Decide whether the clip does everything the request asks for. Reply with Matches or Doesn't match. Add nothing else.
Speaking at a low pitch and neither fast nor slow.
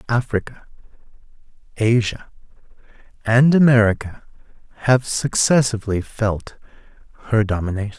Doesn't match